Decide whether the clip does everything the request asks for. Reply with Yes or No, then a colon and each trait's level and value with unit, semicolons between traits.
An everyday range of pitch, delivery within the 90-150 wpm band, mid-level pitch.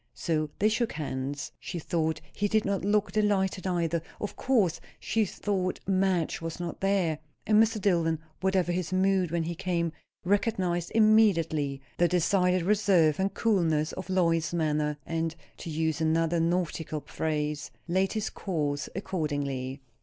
Yes: average, 3.4 semitones; average, 145 wpm; medium, 175 Hz